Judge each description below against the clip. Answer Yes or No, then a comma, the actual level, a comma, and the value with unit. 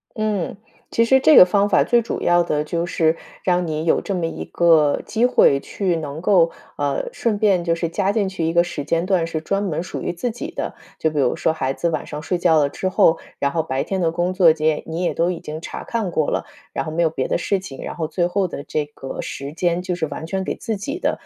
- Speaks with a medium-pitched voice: Yes, medium, 170 Hz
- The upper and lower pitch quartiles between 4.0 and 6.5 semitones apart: No, average, 3.4 semitones